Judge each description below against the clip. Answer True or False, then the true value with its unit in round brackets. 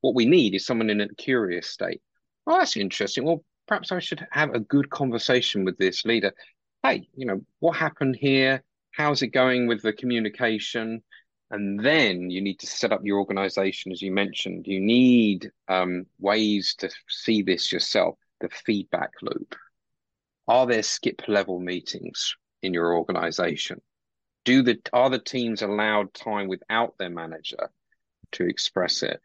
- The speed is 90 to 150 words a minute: False (160 wpm)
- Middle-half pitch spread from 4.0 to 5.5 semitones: True (4.9 semitones)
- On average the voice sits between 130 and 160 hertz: False (110 Hz)